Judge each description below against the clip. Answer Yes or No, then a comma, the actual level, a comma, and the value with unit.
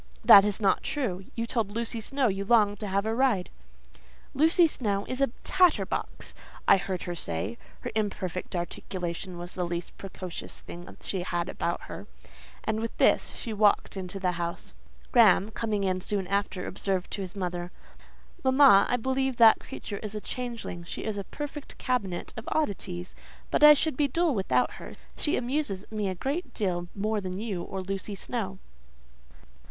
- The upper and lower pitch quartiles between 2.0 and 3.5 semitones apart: No, average, 4.5 semitones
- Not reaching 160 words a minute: No, average, 175 wpm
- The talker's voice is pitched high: Yes, high, 200 Hz